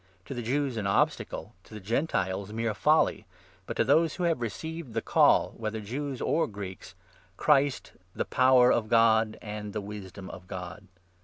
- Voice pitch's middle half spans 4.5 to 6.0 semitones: Yes, average, 4.9 semitones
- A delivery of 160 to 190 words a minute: Yes, average, 180 wpm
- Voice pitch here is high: No, low, 110 Hz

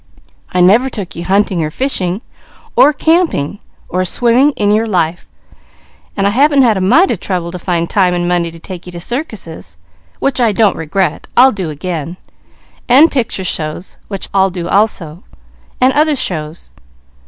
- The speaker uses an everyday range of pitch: No, wide, 5.7 semitones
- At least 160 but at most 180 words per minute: Yes, average, 170 wpm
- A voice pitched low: No, high, 190 Hz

